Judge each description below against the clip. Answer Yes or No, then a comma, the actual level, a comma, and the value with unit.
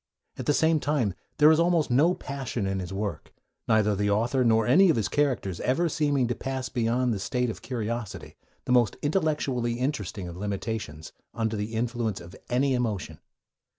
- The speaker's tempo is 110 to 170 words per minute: No, average, 185 wpm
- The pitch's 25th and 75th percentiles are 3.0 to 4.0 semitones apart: No, average, 4.8 semitones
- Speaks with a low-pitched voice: Yes, low, 120 Hz